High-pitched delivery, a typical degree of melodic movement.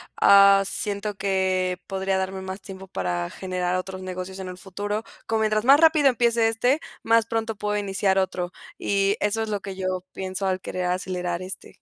No: high, 195 Hz; narrow, 2.2 semitones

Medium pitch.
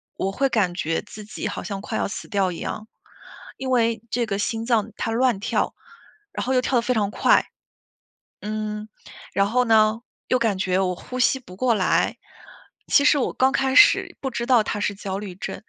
No: high, 220 Hz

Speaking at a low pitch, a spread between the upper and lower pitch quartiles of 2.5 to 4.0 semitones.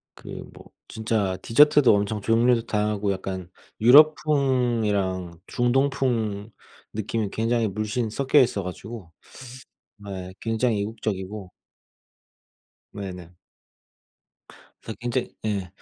Yes: low, 110 Hz; average, 3.5 semitones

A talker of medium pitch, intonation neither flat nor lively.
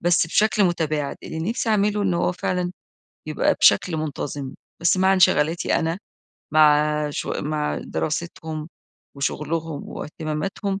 Yes: medium, 165 Hz; average, 3.2 semitones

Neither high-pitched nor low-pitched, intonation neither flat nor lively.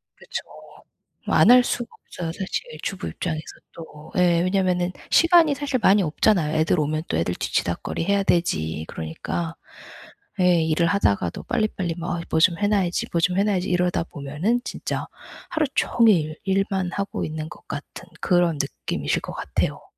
Yes: medium, 175 Hz; average, 3.9 semitones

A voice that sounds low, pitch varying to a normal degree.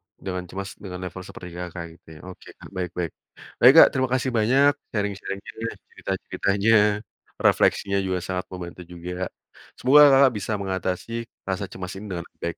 Yes: very low, 95 Hz; average, 3.9 semitones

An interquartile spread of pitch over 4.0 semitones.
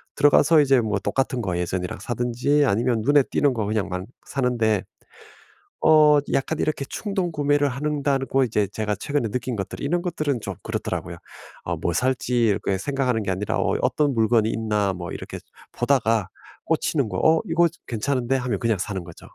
Yes: average, 5.3 semitones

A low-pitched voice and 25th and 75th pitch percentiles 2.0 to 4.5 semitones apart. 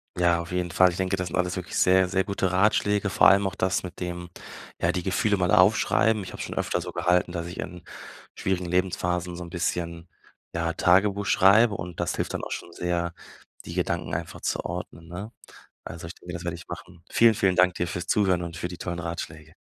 No: very low, 90 Hz; narrow, 1.6 semitones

